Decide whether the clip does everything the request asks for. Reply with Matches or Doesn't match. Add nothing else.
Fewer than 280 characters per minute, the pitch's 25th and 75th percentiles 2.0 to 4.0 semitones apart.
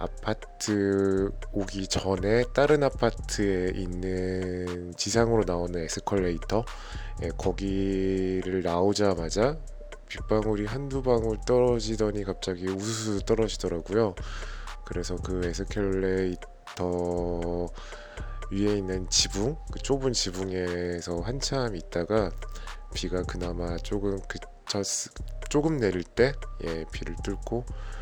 Matches